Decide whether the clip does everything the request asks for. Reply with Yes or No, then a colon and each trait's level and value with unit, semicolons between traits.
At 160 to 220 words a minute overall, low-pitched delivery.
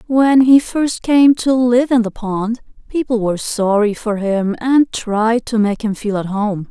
No: average, 195 wpm; high, 230 Hz